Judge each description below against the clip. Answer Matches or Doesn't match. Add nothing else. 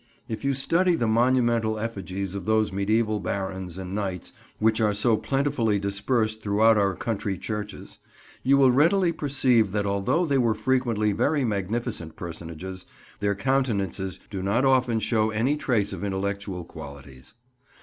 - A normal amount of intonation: Matches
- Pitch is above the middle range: Doesn't match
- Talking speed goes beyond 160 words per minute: Doesn't match